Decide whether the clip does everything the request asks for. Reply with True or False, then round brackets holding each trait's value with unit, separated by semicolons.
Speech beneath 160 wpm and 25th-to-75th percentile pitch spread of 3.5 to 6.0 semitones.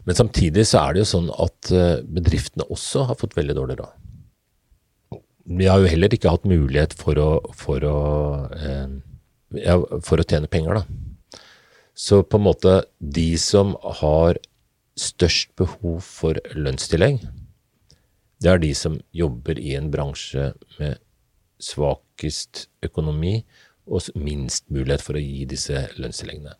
True (140 wpm; 4.2 semitones)